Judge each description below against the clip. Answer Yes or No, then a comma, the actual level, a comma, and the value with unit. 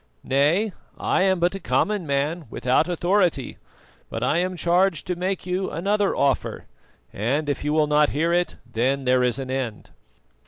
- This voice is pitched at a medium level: Yes, medium, 155 Hz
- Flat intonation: No, average, 4.9 semitones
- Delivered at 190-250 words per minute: No, average, 170 wpm